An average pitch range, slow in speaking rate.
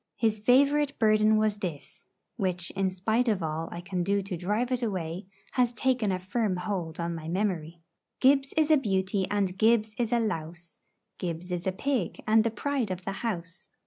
No: average, 4.3 semitones; average, 190 wpm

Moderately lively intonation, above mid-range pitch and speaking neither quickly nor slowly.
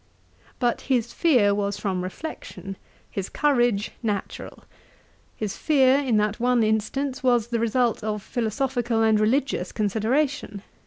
No: average, 3.6 semitones; high, 230 Hz; slow, 125 wpm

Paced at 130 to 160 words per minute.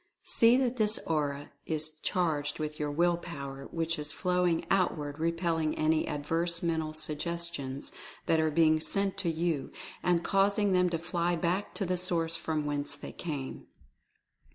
Yes: average, 155 wpm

